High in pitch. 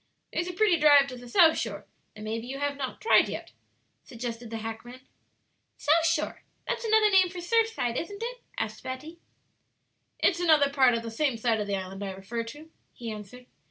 Yes: very high, 260 Hz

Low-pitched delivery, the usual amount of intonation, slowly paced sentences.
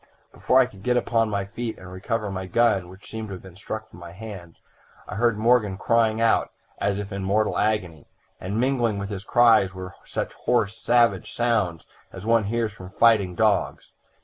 No: low, 105 Hz; average, 3.4 semitones; average, 195 wpm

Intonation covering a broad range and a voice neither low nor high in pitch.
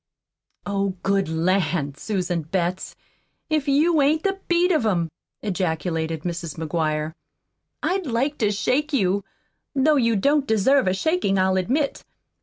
No: wide, 8.4 semitones; high, 200 Hz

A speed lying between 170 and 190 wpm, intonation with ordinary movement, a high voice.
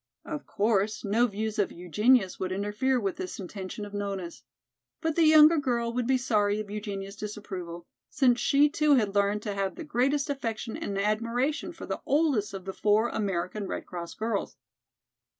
Yes: average, 175 wpm; average, 4.2 semitones; high, 215 Hz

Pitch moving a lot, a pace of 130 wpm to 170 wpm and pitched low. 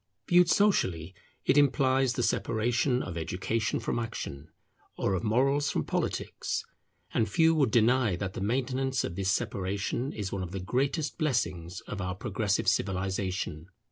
Yes: wide, 5.8 semitones; average, 150 wpm; low, 110 Hz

